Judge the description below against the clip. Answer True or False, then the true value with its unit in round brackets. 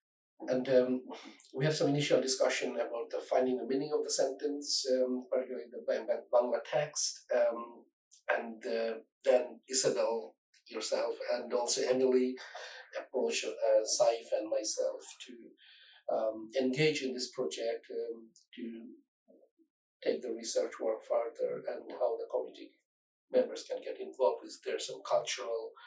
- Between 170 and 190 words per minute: False (135 wpm)